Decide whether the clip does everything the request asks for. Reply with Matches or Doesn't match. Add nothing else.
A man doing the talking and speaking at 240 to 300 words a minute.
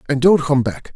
Matches